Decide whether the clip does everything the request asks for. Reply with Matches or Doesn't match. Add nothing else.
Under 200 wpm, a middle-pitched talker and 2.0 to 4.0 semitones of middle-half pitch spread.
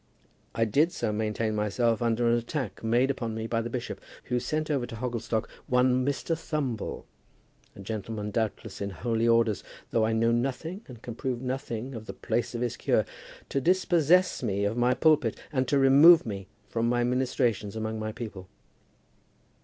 Doesn't match